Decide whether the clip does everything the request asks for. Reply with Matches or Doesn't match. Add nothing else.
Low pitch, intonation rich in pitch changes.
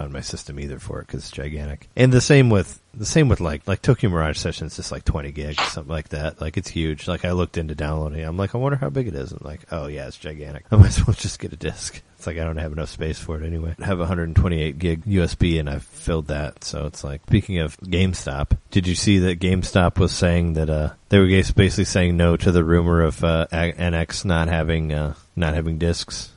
Doesn't match